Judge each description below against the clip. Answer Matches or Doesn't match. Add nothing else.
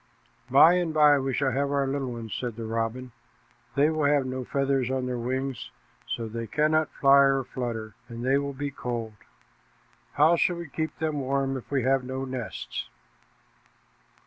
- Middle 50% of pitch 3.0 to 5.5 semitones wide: Doesn't match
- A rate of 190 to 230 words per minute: Doesn't match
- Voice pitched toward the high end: Doesn't match